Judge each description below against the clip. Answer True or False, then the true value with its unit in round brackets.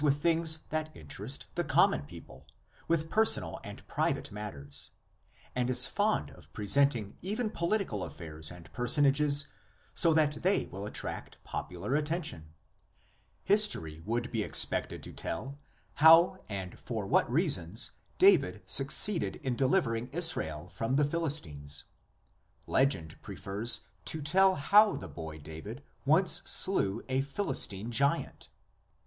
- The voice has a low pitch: True (130 Hz)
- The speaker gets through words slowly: True (130 wpm)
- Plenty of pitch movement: True (8.8 semitones)